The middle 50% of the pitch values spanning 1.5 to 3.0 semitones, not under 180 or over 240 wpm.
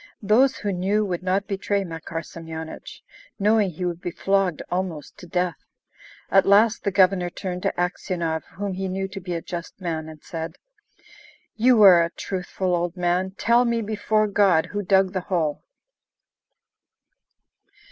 No: narrow, 2.6 semitones; average, 155 wpm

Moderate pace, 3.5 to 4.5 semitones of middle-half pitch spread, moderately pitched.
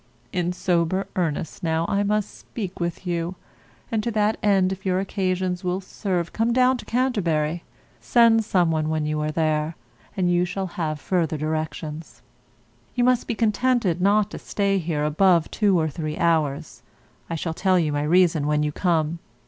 Yes: average, 175 wpm; average, 3.9 semitones; medium, 175 Hz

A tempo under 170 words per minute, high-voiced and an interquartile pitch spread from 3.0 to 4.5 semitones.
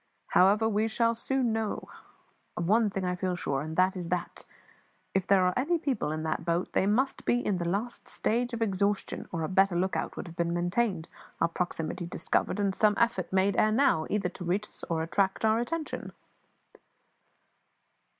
No: average, 195 wpm; high, 195 Hz; average, 4.0 semitones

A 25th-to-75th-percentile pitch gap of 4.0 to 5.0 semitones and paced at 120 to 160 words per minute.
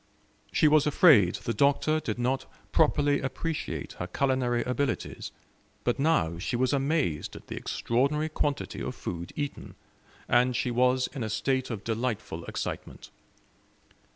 No: average, 3.6 semitones; average, 140 wpm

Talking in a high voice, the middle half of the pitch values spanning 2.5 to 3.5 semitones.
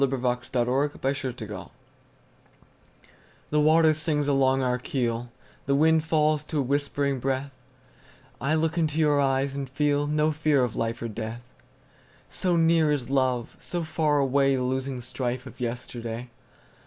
No: low, 135 Hz; average, 2.9 semitones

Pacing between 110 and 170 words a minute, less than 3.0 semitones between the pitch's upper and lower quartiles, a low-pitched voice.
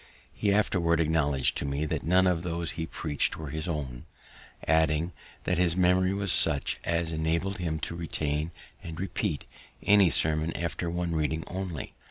Yes: average, 165 wpm; narrow, 2.5 semitones; very low, 85 Hz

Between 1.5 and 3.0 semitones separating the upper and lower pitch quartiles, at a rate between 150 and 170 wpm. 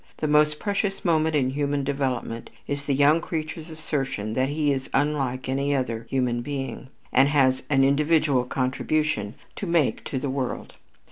Yes: average, 2.7 semitones; average, 160 wpm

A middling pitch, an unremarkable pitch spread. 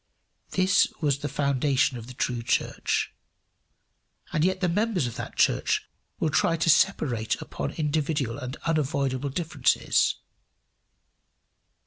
Yes: medium, 145 Hz; average, 4.3 semitones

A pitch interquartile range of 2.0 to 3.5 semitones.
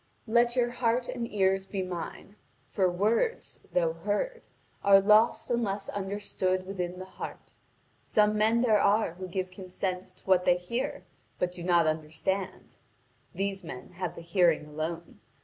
Yes: average, 3.0 semitones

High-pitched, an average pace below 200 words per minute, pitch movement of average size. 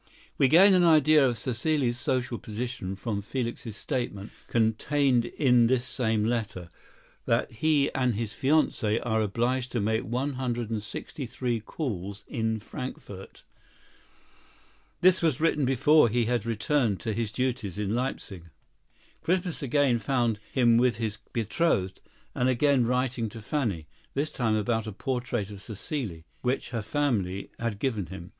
No: low, 120 Hz; average, 145 wpm; average, 3.5 semitones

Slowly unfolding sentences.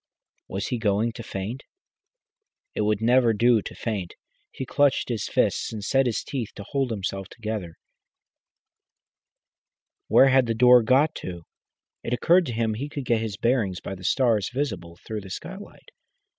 No: average, 165 wpm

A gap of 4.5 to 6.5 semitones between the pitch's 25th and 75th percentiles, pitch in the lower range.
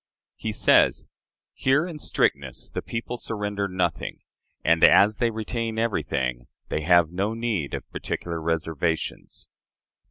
Yes: wide, 5.6 semitones; low, 100 Hz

